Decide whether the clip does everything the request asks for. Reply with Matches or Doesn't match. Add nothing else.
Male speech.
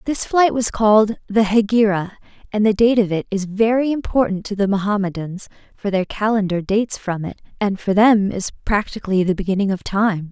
Doesn't match